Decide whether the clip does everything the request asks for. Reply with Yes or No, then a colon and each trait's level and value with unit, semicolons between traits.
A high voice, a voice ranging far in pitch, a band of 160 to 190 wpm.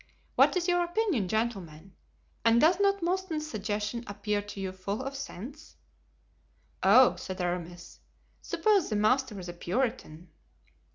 No: high, 220 Hz; wide, 8.3 semitones; average, 145 wpm